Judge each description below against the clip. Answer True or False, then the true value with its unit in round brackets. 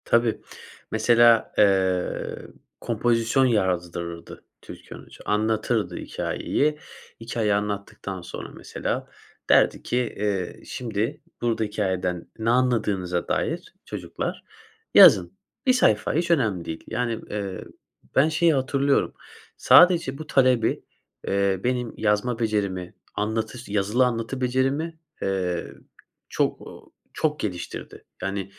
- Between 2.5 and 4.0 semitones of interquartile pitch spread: False (4.4 semitones)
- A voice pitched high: False (110 Hz)